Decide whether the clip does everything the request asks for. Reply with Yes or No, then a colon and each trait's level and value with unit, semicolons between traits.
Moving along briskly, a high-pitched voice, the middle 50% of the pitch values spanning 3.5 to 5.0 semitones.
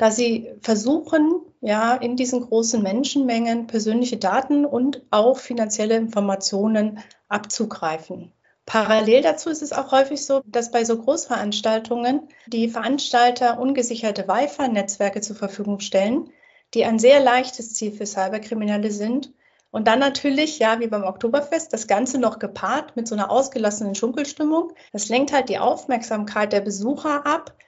No: average, 140 wpm; high, 235 Hz; average, 4.1 semitones